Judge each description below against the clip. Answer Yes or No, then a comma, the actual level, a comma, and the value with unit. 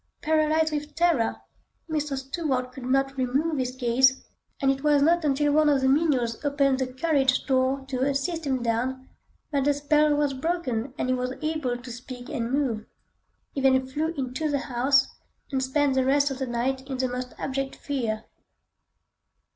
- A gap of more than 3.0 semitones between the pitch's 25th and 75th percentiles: No, narrow, 2.4 semitones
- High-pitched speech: Yes, very high, 270 Hz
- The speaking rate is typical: Yes, average, 180 wpm